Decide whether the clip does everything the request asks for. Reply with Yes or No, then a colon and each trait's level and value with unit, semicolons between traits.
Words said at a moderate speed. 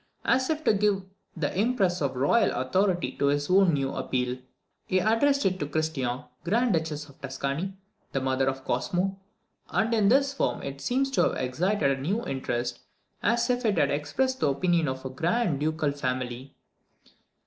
Yes: average, 170 wpm